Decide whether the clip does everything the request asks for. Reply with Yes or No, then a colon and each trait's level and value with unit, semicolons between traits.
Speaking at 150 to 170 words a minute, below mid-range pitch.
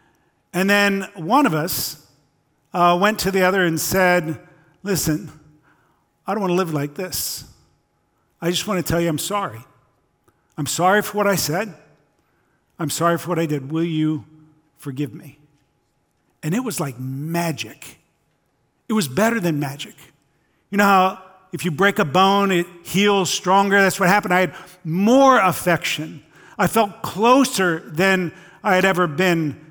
No: average, 160 wpm; medium, 175 Hz